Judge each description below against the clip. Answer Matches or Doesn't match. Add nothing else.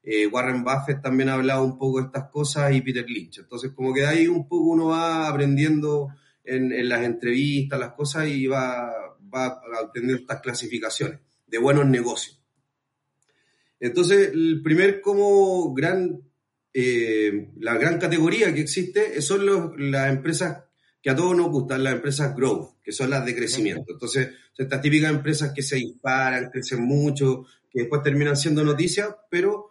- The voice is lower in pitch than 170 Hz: Matches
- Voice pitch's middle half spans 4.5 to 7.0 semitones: Doesn't match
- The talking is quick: Doesn't match